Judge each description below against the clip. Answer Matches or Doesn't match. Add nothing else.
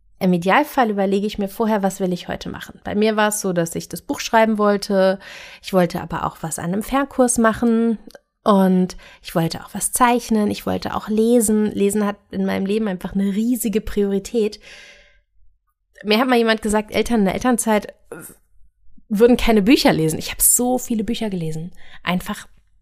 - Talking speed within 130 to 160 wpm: Doesn't match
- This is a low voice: Doesn't match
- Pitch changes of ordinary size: Matches